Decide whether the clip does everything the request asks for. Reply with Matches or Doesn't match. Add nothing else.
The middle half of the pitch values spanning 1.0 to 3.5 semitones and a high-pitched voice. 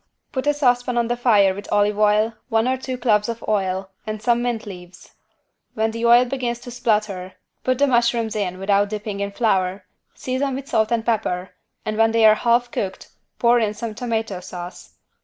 Matches